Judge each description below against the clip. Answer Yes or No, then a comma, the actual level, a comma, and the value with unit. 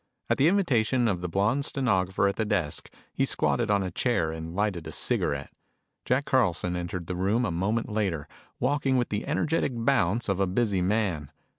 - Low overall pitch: Yes, low, 100 Hz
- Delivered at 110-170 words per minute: No, average, 185 wpm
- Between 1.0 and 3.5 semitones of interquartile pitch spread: No, average, 5.3 semitones